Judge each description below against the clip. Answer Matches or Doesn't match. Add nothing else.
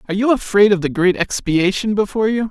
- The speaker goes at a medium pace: Doesn't match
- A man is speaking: Matches